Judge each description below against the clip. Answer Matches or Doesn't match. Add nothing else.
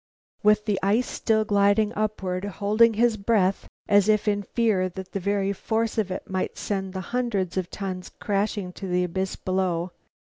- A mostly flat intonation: Matches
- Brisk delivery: Doesn't match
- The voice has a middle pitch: Doesn't match